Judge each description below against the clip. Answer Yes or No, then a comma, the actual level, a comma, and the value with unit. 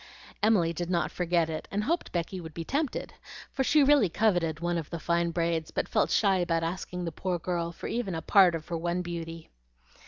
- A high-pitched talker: No, medium, 175 Hz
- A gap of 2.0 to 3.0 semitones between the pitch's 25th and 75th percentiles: Yes, narrow, 2.4 semitones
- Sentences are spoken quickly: Yes, fast, 215 wpm